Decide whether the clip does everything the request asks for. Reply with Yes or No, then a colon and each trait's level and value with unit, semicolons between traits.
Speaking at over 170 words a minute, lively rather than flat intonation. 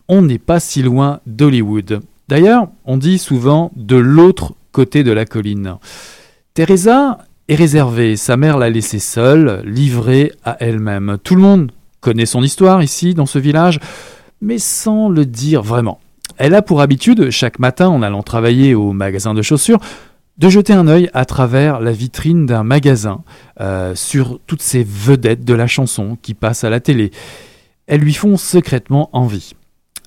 No: average, 165 wpm; wide, 6.3 semitones